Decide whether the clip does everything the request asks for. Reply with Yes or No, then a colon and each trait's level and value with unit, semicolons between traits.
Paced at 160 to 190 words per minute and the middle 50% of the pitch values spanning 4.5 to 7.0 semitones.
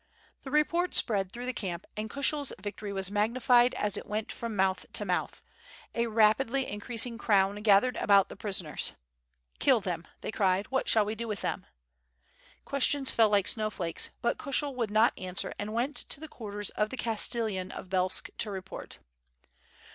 No: average, 175 wpm; average, 3.5 semitones